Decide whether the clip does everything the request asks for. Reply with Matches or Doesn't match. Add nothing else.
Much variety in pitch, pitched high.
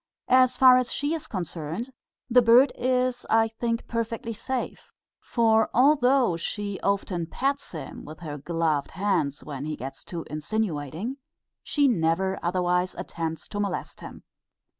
Matches